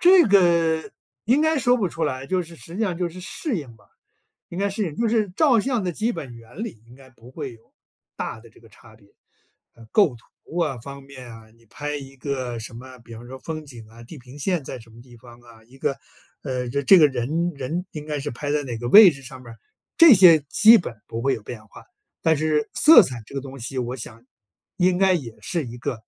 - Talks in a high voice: No, medium, 140 Hz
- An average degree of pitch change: No, wide, 6.8 semitones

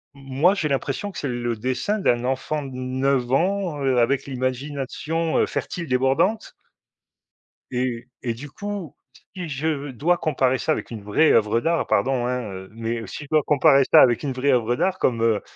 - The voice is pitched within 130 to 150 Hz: Yes, low, 135 Hz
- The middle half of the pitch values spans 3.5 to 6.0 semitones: Yes, average, 3.9 semitones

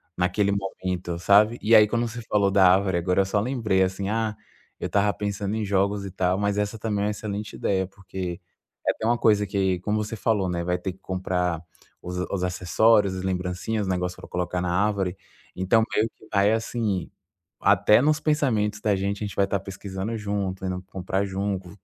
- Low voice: Yes, low, 100 Hz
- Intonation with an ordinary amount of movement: No, narrow, 2.2 semitones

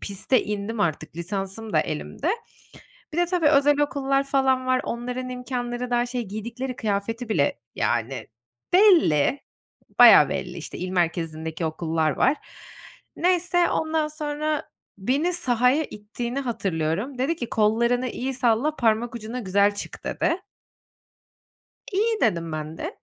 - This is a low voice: No, high, 240 Hz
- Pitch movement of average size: No, wide, 5.9 semitones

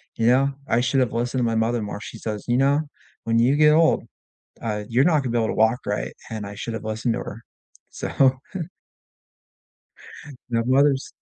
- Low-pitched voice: Yes, low, 120 Hz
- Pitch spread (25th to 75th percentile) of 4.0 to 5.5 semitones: No, average, 3.1 semitones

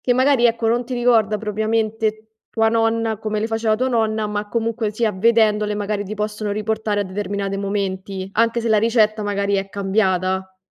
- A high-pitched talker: Yes, high, 215 Hz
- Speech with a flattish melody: Yes, narrow, 1.8 semitones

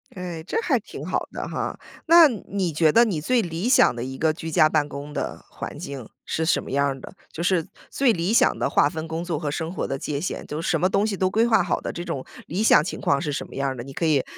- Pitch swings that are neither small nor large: Yes, average, 4.6 semitones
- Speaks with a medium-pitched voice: Yes, medium, 160 Hz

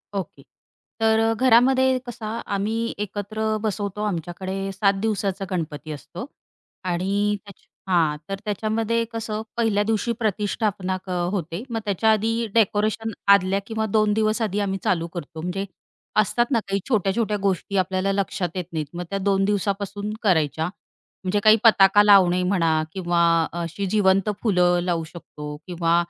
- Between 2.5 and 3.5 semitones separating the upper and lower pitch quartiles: Yes, average, 3.1 semitones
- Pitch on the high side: Yes, high, 200 Hz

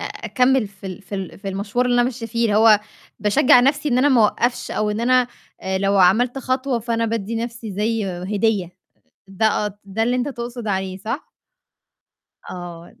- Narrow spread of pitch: No, average, 3.6 semitones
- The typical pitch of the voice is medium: No, high, 220 Hz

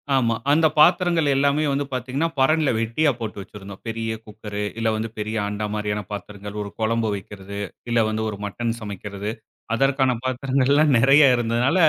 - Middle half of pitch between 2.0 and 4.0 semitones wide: No, average, 4.7 semitones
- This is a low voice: Yes, low, 115 Hz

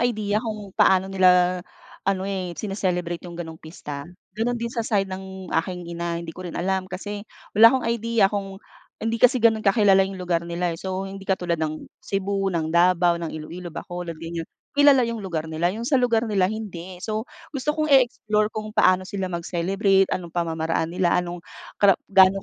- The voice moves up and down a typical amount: Yes, average, 3.5 semitones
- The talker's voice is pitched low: No, high, 190 Hz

